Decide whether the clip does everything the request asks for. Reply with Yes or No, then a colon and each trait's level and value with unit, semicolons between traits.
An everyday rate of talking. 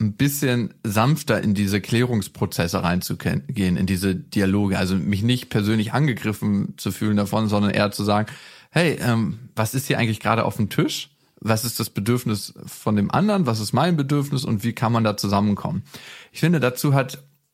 Yes: average, 180 wpm